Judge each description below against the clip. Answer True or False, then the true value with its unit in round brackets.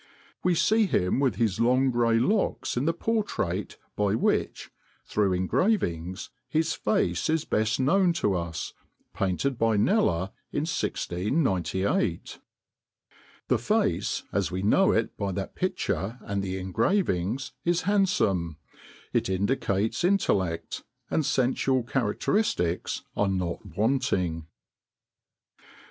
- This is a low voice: True (110 Hz)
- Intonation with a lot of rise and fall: True (8.9 semitones)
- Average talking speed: False (115 wpm)